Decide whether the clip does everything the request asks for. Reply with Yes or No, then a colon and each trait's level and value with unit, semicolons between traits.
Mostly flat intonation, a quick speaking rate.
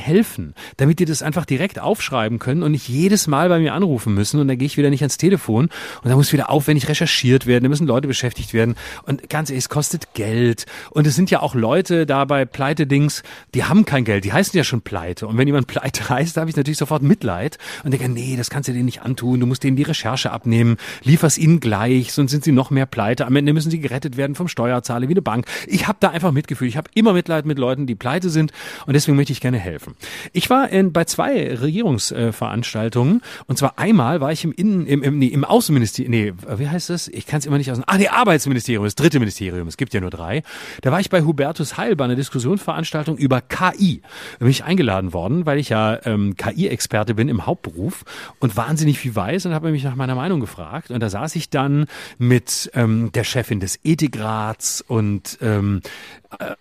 No: average, 4.7 semitones; fast, 225 wpm